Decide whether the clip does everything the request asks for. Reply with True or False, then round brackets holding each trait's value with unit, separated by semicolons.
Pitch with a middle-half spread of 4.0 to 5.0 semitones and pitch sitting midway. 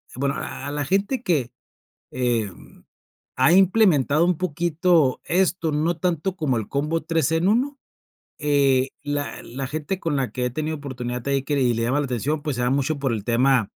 True (4.4 semitones; 145 Hz)